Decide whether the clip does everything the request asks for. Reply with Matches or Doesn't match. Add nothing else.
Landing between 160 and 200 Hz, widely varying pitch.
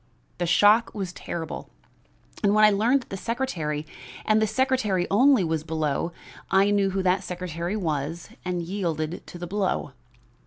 Doesn't match